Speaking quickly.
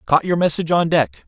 Yes: fast, 235 wpm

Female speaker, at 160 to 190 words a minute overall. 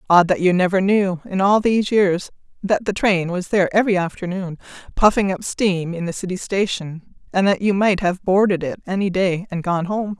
No: female; fast, 205 wpm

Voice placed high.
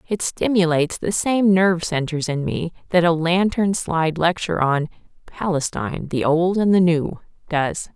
No: medium, 170 Hz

